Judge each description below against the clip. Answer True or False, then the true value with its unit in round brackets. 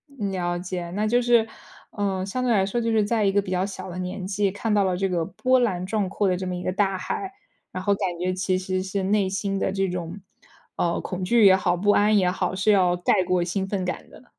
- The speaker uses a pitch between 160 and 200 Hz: True (190 Hz)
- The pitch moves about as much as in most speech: False (2.0 semitones)